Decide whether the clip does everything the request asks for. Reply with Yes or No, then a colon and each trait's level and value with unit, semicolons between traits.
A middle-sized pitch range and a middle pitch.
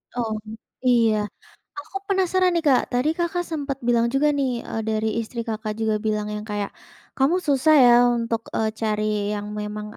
No: average, 5.0 semitones; high, 235 Hz